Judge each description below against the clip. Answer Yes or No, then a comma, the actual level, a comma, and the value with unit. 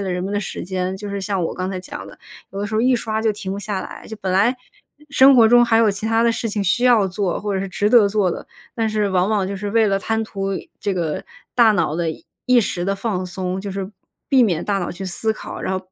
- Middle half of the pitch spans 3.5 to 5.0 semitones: No, average, 2.8 semitones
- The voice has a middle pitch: No, high, 200 Hz